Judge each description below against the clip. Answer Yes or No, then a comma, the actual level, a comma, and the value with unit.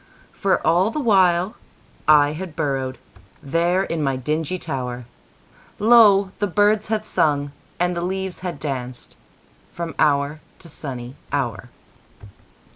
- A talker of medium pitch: Yes, medium, 160 Hz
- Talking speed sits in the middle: No, slow, 115 wpm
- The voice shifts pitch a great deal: Yes, wide, 5.7 semitones